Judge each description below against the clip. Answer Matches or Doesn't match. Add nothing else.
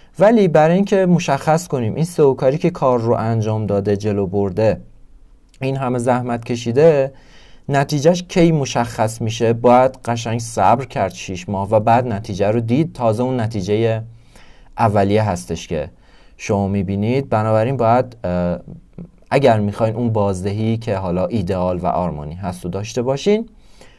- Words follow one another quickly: Doesn't match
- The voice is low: Matches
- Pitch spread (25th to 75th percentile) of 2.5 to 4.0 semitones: Doesn't match